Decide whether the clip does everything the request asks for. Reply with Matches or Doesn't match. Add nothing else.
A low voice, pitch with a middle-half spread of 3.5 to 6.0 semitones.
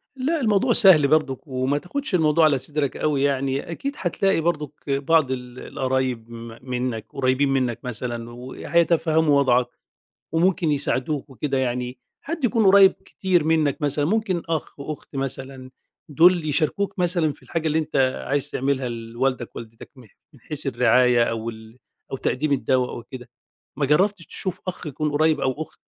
Doesn't match